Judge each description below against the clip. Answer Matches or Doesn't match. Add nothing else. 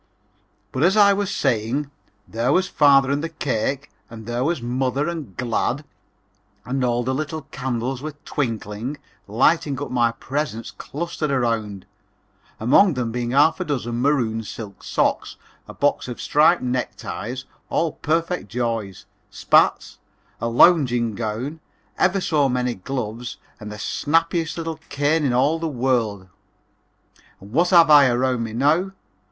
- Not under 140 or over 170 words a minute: Matches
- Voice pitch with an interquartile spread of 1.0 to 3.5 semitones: Doesn't match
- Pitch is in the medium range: Doesn't match